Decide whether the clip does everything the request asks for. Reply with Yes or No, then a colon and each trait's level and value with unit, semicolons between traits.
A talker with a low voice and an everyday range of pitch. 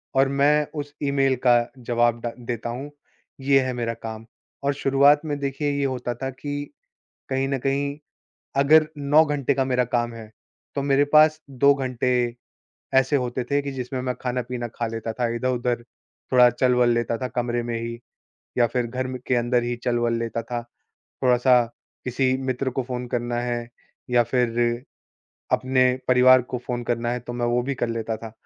No: low, 125 Hz; narrow, 2.3 semitones